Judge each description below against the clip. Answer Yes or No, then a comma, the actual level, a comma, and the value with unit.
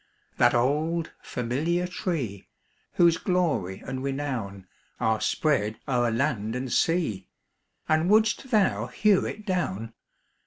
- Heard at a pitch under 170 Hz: Yes, medium, 140 Hz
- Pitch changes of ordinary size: No, wide, 7.3 semitones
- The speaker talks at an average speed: No, slow, 115 wpm